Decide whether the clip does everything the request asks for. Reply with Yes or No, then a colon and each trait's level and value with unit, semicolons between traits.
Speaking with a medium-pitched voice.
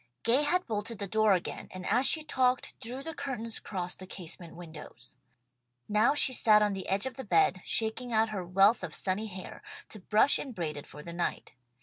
No: high, 210 Hz